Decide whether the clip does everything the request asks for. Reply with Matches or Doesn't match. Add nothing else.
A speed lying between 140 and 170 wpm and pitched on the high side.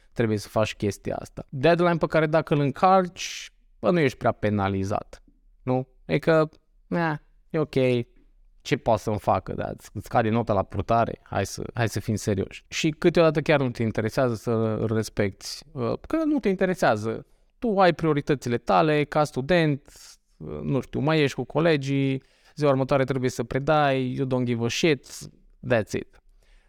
Doesn't match